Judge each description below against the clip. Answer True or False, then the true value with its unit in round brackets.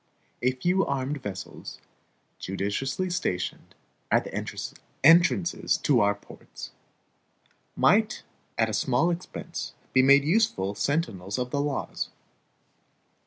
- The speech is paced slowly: True (110 wpm)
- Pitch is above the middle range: False (135 Hz)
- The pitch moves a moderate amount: False (8.3 semitones)